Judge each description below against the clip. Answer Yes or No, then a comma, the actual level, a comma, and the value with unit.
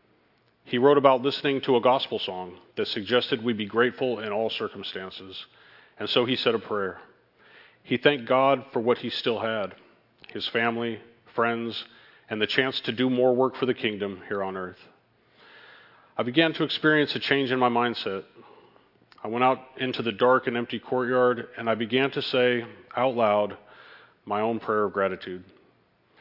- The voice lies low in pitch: Yes, low, 120 Hz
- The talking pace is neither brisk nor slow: Yes, average, 175 wpm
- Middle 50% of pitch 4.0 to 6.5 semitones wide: No, average, 3.4 semitones